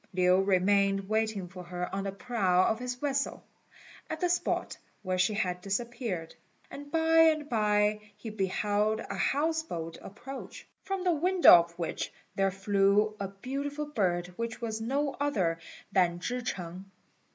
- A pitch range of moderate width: No, wide, 6.5 semitones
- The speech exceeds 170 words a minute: No, average, 155 wpm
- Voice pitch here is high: Yes, high, 210 Hz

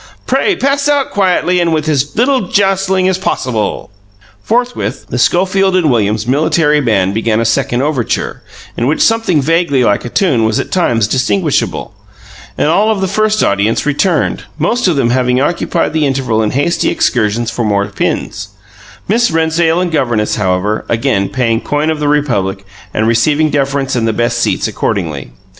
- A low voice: No, medium, 145 Hz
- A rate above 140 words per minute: Yes, average, 170 wpm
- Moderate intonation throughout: No, wide, 7.7 semitones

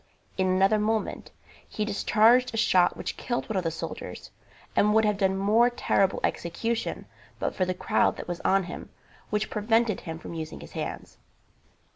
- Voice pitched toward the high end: Yes, high, 205 Hz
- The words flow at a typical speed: Yes, average, 175 wpm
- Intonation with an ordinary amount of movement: Yes, average, 3.1 semitones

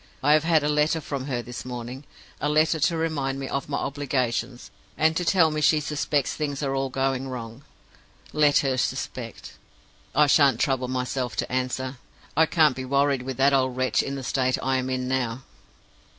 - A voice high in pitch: No, low, 135 Hz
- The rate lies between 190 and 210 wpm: Yes, average, 195 wpm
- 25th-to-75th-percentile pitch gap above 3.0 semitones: No, narrow, 2.5 semitones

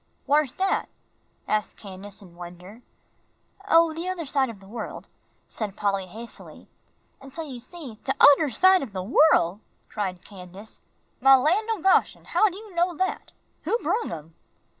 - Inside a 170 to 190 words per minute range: No, average, 160 wpm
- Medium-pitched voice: No, very high, 255 Hz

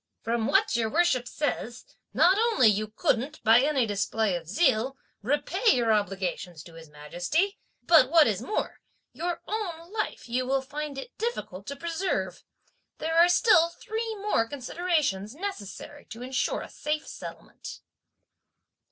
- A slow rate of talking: No, average, 145 wpm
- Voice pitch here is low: No, very high, 270 Hz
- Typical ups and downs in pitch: No, wide, 7.7 semitones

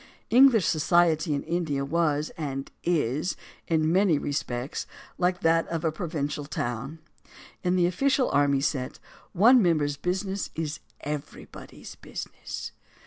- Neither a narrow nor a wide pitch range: Yes, average, 3.6 semitones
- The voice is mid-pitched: Yes, medium, 160 Hz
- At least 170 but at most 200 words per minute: No, slow, 135 wpm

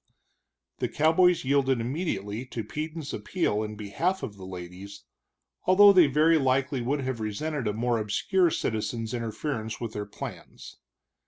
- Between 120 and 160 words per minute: Yes, average, 145 wpm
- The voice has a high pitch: No, low, 130 Hz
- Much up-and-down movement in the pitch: Yes, wide, 6.4 semitones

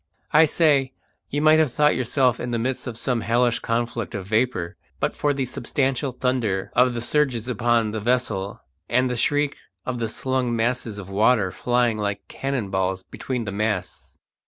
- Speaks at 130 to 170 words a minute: No, average, 180 wpm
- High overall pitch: No, low, 120 Hz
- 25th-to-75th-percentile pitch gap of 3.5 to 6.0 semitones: No, average, 3.0 semitones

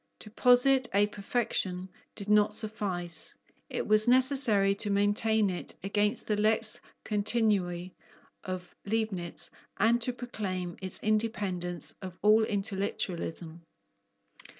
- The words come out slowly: Yes, slow, 110 wpm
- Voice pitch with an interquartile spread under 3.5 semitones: Yes, average, 2.9 semitones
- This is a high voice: Yes, high, 205 Hz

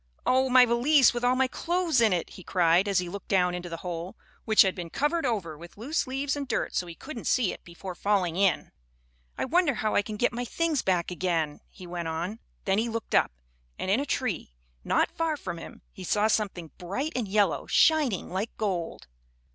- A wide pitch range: Yes, wide, 6.3 semitones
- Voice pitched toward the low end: No, high, 205 Hz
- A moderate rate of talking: No, fast, 215 wpm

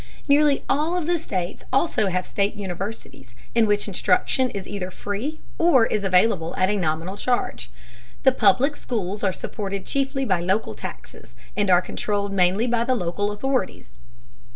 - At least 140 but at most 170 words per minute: Yes, average, 160 wpm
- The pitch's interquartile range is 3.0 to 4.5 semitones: No, wide, 5.5 semitones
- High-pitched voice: Yes, high, 205 Hz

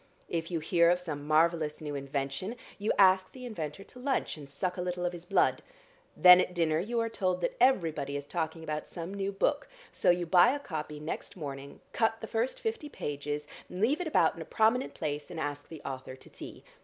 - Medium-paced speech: No, fast, 215 wpm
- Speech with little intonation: No, average, 5.0 semitones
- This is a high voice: No, medium, 175 Hz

